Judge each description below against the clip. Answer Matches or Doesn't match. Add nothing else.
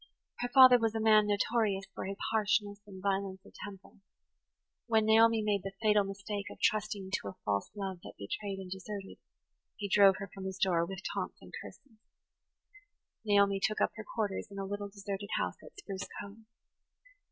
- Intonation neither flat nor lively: Doesn't match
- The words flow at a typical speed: Matches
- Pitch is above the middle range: Matches